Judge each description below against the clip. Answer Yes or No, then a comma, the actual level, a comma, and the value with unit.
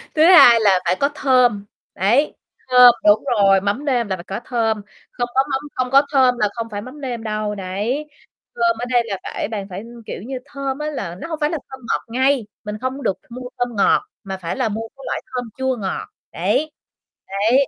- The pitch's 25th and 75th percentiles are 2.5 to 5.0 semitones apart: Yes, average, 4.3 semitones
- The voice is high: Yes, high, 240 Hz